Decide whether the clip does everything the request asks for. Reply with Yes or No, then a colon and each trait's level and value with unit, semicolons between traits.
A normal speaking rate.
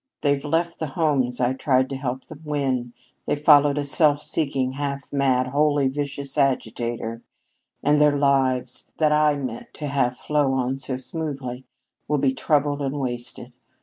Yes: average, 160 wpm